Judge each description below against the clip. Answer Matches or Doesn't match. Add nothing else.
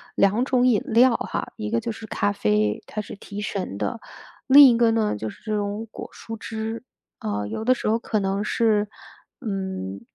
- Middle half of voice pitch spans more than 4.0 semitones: Doesn't match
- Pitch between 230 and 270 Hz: Doesn't match